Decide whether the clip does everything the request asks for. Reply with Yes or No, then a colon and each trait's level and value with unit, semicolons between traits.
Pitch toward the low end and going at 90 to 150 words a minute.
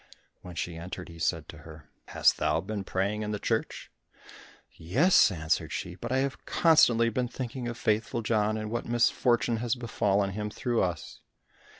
No: low, 105 Hz; average, 175 wpm